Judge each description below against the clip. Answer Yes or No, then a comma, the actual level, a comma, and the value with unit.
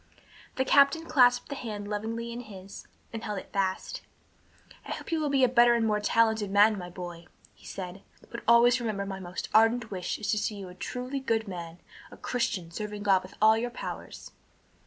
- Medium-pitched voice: No, high, 215 Hz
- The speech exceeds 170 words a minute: Yes, average, 200 wpm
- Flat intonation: No, average, 3.6 semitones